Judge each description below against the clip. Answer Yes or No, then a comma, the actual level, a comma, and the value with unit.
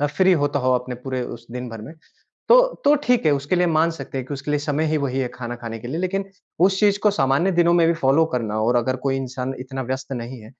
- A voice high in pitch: No, low, 135 Hz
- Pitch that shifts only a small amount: No, average, 4.6 semitones